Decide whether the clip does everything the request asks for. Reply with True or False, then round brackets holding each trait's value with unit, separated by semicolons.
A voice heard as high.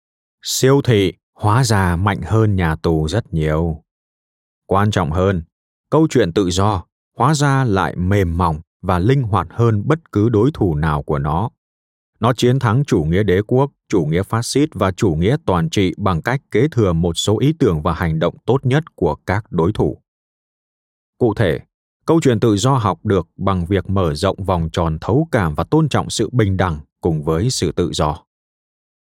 False (100 Hz)